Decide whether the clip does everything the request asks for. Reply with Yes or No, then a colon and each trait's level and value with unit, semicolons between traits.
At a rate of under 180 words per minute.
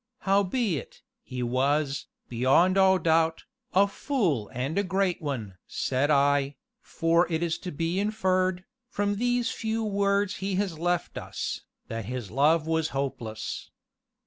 Yes: average, 140 wpm